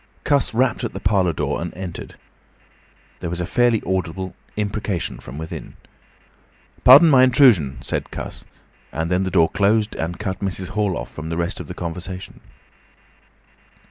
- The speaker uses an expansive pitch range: No, average, 4.0 semitones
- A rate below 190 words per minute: Yes, average, 160 wpm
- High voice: No, very low, 95 Hz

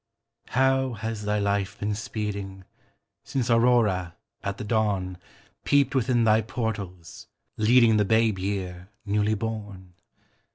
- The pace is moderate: No, slow, 120 wpm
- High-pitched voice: No, low, 105 Hz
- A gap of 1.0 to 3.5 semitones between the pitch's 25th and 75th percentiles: Yes, narrow, 2.6 semitones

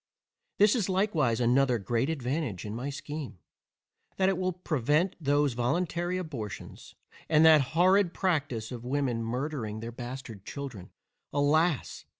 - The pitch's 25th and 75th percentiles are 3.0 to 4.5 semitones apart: No, wide, 5.6 semitones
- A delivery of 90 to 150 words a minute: Yes, slow, 135 wpm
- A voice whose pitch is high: No, medium, 145 Hz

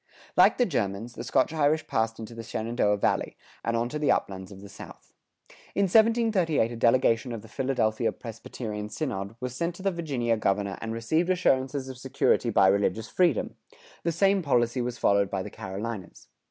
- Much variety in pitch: Yes, wide, 5.7 semitones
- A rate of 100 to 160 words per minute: No, average, 180 wpm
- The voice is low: Yes, low, 120 Hz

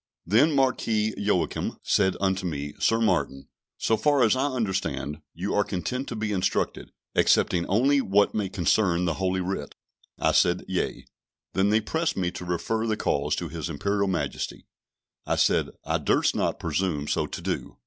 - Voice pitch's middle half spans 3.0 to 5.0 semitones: Yes, average, 4.0 semitones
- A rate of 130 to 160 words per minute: No, average, 170 wpm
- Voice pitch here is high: No, very low, 95 Hz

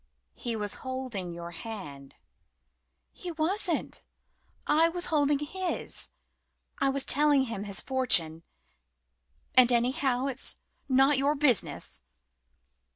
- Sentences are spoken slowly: Yes, slow, 105 wpm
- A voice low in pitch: No, very high, 260 Hz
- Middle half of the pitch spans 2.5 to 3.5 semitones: No, wide, 5.6 semitones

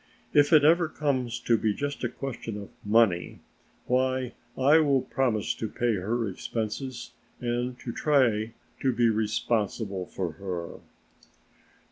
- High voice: No, low, 120 Hz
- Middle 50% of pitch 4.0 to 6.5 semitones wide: No, average, 3.6 semitones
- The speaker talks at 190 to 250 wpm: No, slow, 135 wpm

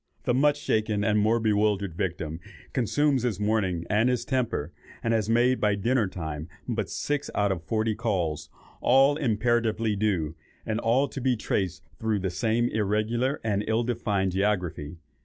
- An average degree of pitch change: Yes, average, 3.7 semitones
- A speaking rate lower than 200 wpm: Yes, average, 160 wpm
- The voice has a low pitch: Yes, low, 110 Hz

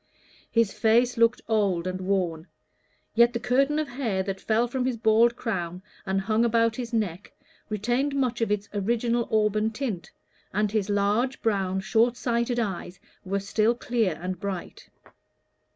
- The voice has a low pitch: No, high, 220 Hz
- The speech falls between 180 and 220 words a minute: No, average, 155 wpm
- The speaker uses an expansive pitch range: No, average, 3.3 semitones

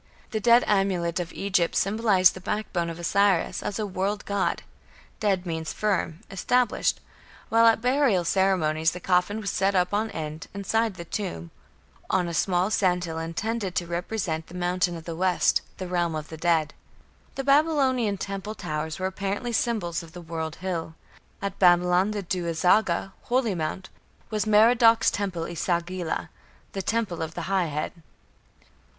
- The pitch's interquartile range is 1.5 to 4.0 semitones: Yes, average, 3.5 semitones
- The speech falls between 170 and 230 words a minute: No, average, 160 wpm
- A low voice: No, medium, 185 Hz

